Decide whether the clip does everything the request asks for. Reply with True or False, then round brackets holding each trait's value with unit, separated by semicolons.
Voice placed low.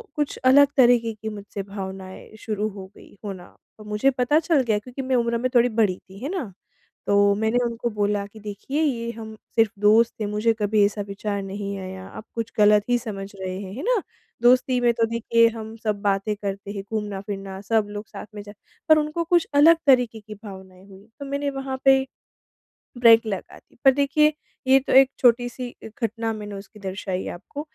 False (220 Hz)